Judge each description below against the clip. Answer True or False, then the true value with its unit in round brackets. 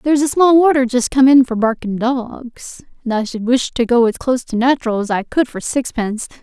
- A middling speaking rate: False (235 wpm)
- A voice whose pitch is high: True (250 Hz)